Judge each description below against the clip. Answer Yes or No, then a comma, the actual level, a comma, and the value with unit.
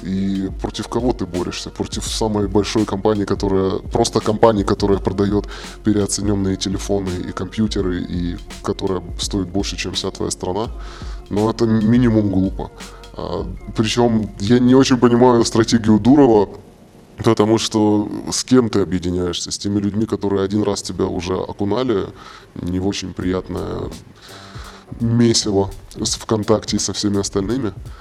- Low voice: Yes, low, 100 Hz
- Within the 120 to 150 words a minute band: Yes, slow, 135 wpm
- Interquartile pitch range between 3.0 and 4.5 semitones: No, narrow, 2.6 semitones